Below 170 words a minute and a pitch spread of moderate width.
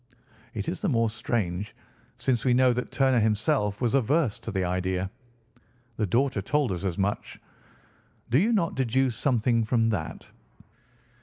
Yes: average, 155 wpm; average, 4.5 semitones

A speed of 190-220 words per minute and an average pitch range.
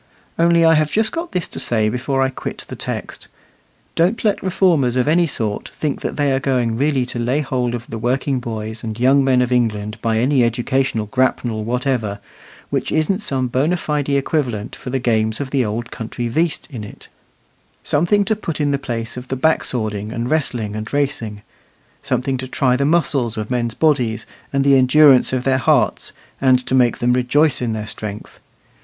Yes: average, 195 wpm; average, 3.8 semitones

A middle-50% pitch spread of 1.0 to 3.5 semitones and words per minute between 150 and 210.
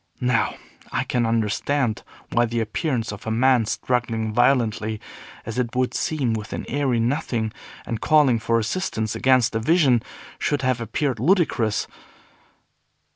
No: average, 2.9 semitones; average, 140 wpm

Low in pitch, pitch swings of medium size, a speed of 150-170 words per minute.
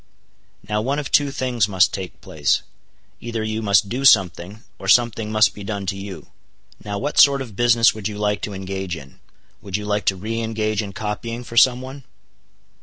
No: low, 105 Hz; average, 3.0 semitones; average, 195 wpm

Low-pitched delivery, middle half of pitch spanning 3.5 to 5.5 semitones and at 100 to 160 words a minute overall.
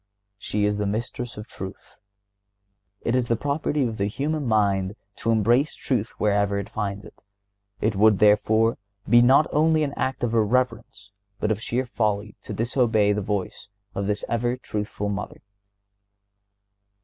No: low, 110 Hz; average, 3.0 semitones; average, 155 wpm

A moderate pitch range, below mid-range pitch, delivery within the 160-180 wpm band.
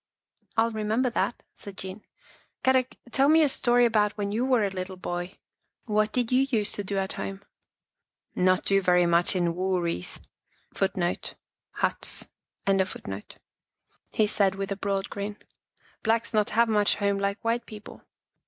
No: average, 3.1 semitones; high, 205 Hz; average, 165 wpm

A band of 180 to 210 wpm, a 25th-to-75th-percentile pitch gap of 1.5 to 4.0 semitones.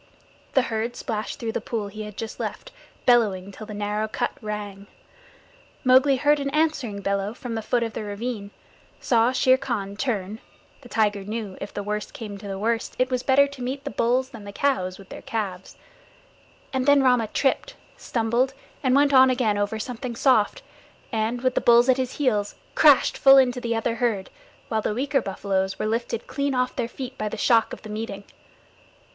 Yes: average, 195 wpm; average, 3.6 semitones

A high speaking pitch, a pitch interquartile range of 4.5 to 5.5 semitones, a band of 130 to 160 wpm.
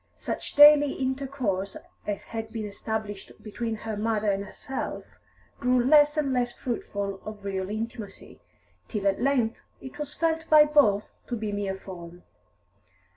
Yes: high, 225 Hz; average, 4.9 semitones; average, 145 wpm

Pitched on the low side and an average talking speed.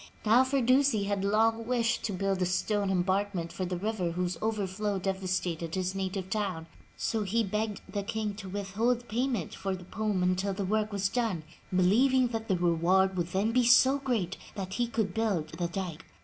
No: high, 200 Hz; average, 190 wpm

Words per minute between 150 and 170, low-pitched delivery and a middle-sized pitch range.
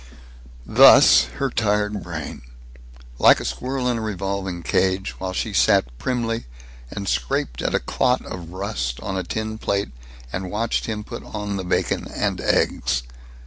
Yes: average, 155 wpm; low, 100 Hz; average, 3.4 semitones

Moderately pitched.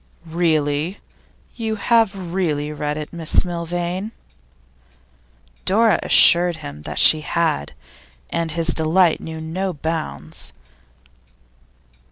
Yes: medium, 165 Hz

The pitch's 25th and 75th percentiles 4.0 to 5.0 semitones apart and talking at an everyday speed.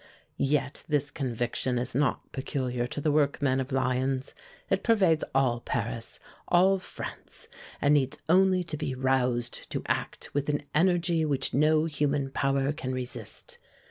No: average, 3.2 semitones; average, 145 wpm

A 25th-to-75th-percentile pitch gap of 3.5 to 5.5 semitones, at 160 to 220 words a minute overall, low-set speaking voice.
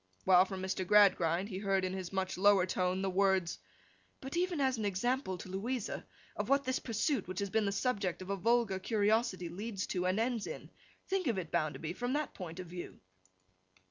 No: average, 4.0 semitones; fast, 205 wpm; high, 195 Hz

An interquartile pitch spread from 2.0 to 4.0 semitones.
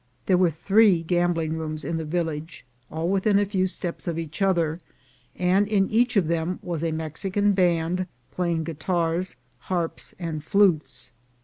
Yes: average, 2.7 semitones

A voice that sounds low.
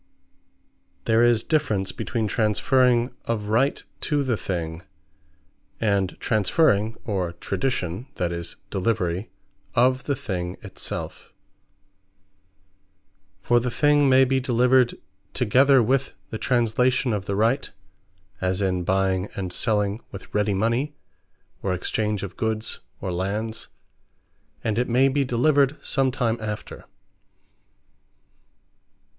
Yes: low, 110 Hz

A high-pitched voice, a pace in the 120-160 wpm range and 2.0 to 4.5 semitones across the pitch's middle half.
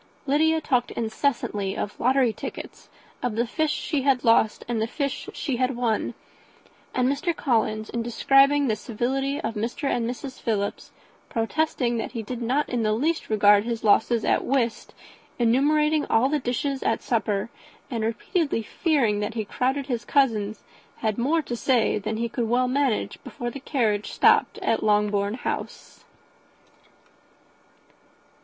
Yes: high, 240 Hz; average, 155 wpm; average, 3.8 semitones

